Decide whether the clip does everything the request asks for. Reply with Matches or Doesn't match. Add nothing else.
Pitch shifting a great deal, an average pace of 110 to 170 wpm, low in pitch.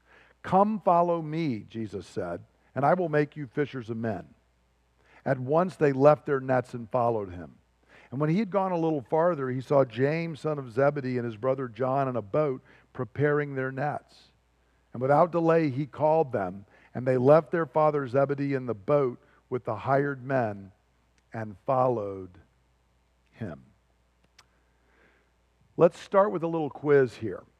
Matches